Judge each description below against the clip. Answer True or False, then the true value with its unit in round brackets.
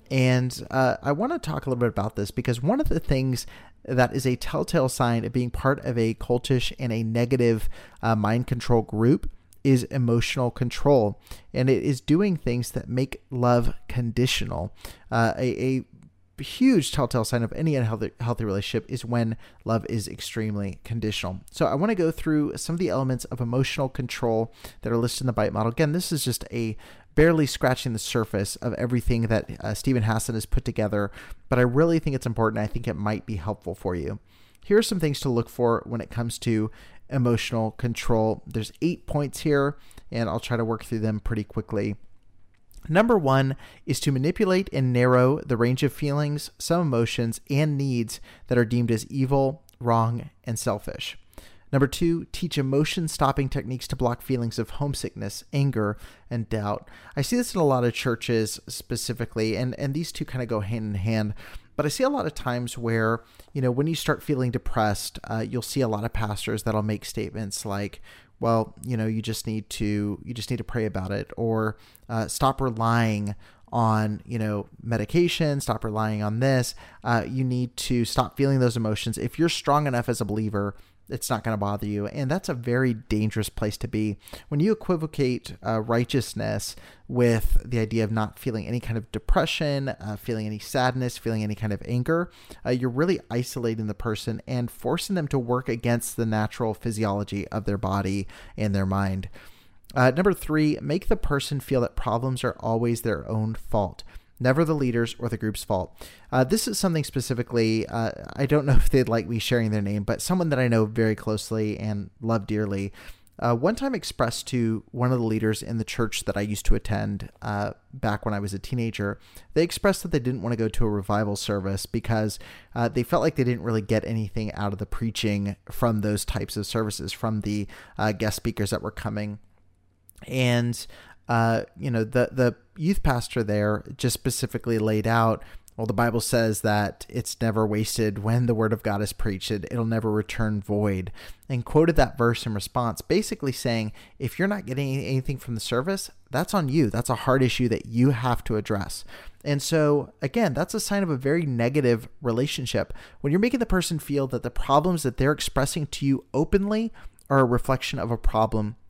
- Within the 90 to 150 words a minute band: False (200 wpm)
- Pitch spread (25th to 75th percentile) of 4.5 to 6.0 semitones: False (3.6 semitones)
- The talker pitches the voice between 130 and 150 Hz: False (115 Hz)